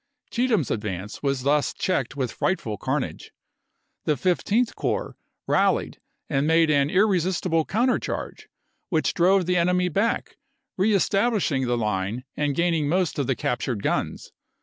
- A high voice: No, medium, 160 Hz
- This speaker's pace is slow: No, average, 150 wpm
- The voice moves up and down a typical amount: No, wide, 6.0 semitones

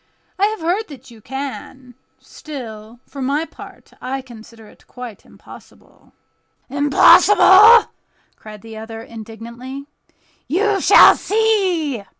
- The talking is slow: Yes, slow, 115 wpm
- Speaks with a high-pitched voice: Yes, very high, 265 Hz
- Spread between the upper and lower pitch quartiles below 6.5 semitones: No, wide, 7.3 semitones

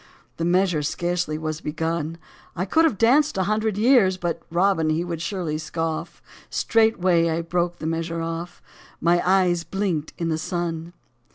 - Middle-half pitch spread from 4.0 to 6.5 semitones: No, narrow, 2.4 semitones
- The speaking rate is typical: Yes, average, 170 wpm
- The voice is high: No, medium, 175 Hz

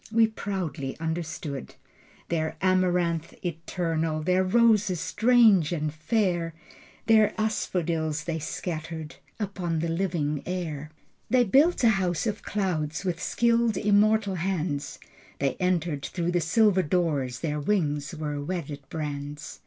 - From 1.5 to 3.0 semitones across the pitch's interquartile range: No, average, 4.1 semitones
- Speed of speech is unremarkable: No, slow, 120 wpm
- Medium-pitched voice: Yes, medium, 170 Hz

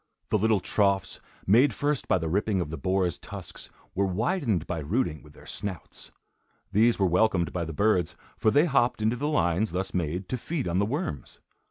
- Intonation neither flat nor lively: Yes, average, 4.4 semitones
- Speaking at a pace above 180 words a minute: Yes, average, 195 wpm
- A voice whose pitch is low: Yes, low, 100 Hz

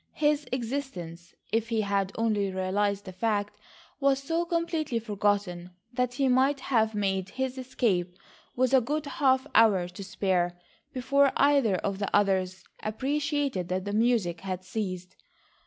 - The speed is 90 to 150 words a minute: Yes, average, 145 wpm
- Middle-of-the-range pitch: No, high, 215 Hz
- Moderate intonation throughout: No, wide, 5.8 semitones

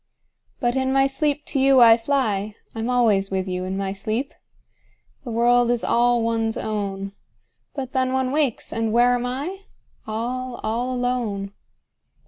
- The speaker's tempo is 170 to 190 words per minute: No, average, 160 wpm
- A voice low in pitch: No, high, 240 Hz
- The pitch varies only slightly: No, average, 3.1 semitones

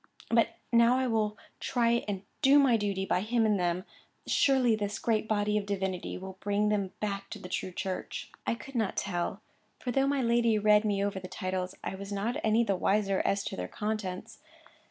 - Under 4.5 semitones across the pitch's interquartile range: Yes, average, 3.1 semitones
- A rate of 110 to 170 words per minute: No, average, 200 wpm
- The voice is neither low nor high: No, high, 210 Hz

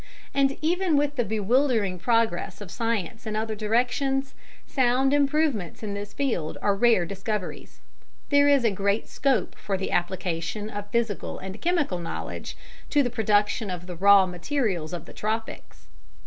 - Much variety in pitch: Yes, wide, 5.7 semitones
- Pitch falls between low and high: No, high, 215 Hz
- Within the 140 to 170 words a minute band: Yes, average, 150 wpm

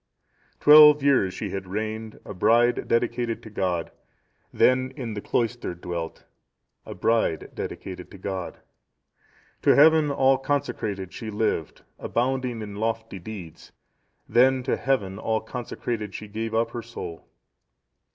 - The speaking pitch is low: Yes, low, 110 Hz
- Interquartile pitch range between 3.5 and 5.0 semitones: Yes, average, 4.0 semitones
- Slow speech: Yes, slow, 130 wpm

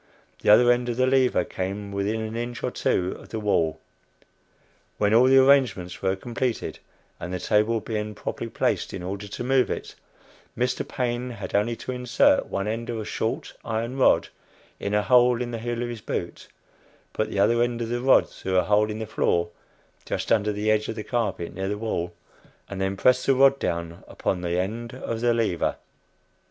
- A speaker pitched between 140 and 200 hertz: No, low, 110 Hz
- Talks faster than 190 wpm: Yes, average, 200 wpm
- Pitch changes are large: No, average, 3.3 semitones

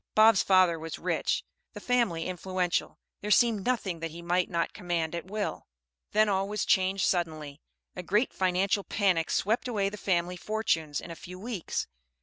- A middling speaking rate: Yes, average, 170 wpm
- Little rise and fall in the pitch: No, average, 3.4 semitones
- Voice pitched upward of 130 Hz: Yes, medium, 185 Hz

